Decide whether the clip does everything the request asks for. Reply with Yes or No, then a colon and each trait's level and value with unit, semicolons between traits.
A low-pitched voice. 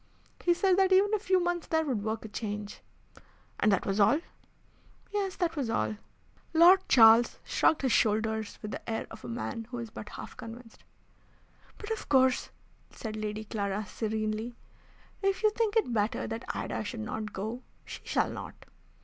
No: high, 225 Hz